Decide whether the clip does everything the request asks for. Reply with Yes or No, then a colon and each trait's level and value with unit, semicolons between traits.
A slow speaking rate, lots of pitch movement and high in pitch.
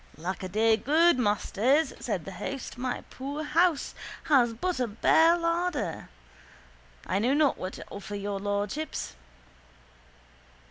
Yes: slow, 125 wpm; wide, 7.2 semitones; very high, 255 Hz